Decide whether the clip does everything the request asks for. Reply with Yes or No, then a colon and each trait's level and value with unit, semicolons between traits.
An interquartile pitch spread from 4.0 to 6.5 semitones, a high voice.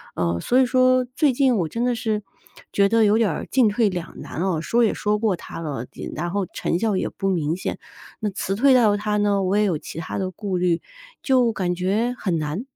Yes: average, 4.5 semitones; high, 205 Hz